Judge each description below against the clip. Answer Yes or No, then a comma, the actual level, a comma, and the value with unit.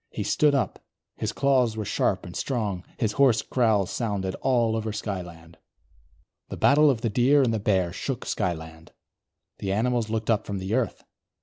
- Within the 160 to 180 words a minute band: Yes, average, 175 wpm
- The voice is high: No, low, 110 Hz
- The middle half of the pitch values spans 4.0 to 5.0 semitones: Yes, average, 4.4 semitones